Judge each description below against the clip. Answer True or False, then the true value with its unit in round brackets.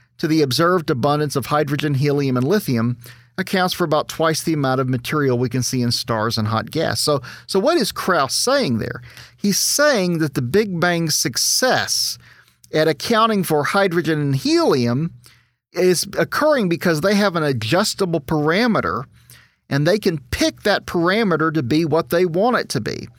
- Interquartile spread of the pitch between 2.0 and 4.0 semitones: False (5.6 semitones)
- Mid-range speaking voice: True (160 Hz)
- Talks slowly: False (175 wpm)